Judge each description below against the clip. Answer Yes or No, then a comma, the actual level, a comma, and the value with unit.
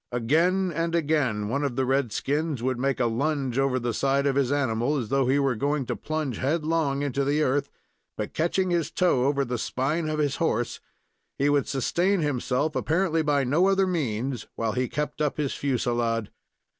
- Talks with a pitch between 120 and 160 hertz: Yes, medium, 140 Hz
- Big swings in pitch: No, average, 3.4 semitones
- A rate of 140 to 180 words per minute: No, average, 195 wpm